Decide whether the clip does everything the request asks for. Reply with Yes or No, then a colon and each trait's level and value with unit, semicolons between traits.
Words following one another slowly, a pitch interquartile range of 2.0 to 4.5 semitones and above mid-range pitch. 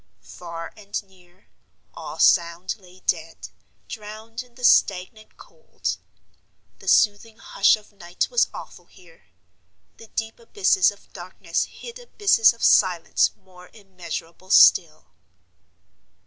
Yes: slow, 120 wpm; average, 4.0 semitones; high, 195 Hz